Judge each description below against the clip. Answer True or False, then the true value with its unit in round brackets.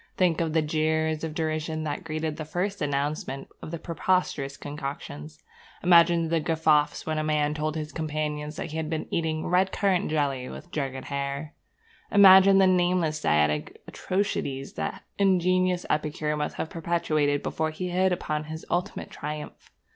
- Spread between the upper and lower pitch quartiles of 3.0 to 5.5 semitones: False (2.5 semitones)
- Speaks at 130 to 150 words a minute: False (160 wpm)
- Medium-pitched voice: True (155 Hz)